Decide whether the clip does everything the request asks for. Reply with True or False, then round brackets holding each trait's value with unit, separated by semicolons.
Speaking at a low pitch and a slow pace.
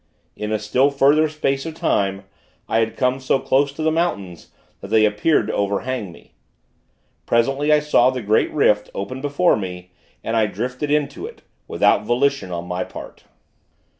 False (125 Hz; 170 wpm)